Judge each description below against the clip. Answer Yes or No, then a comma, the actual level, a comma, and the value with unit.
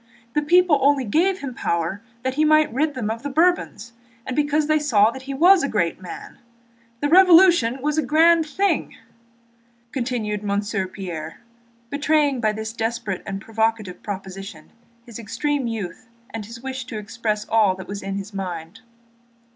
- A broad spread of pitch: Yes, wide, 6.3 semitones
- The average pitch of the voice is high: Yes, high, 235 Hz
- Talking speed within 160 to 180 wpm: Yes, average, 165 wpm